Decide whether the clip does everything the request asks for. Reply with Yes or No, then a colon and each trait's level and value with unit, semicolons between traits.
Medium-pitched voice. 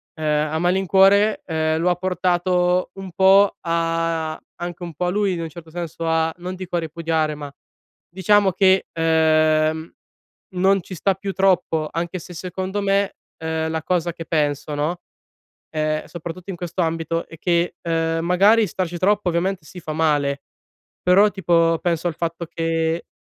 Yes: medium, 170 Hz